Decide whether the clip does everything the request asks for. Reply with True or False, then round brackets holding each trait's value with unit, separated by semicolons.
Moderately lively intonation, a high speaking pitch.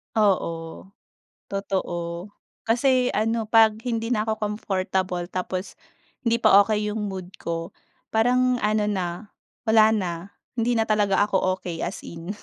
True (3.2 semitones; 210 Hz)